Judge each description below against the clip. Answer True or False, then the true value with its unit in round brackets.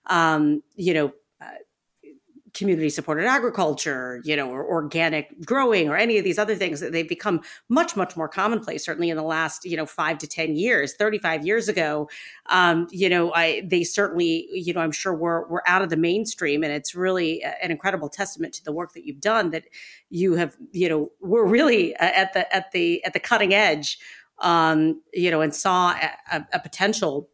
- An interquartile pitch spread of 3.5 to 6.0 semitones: True (3.9 semitones)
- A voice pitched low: False (170 Hz)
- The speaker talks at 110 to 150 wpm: False (200 wpm)